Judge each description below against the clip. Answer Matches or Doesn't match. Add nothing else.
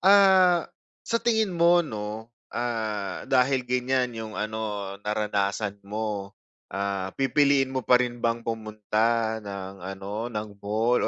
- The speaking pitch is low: Matches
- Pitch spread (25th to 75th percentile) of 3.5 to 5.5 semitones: Matches